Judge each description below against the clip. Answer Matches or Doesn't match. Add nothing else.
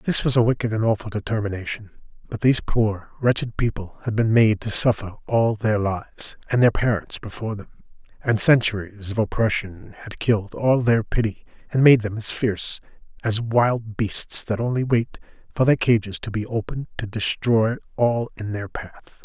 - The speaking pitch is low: Matches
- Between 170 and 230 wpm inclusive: Matches